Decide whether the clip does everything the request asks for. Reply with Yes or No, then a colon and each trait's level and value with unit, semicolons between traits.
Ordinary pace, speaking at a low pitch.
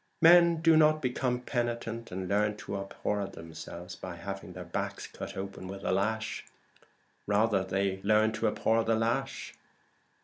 Yes: average, 150 wpm; low, 105 Hz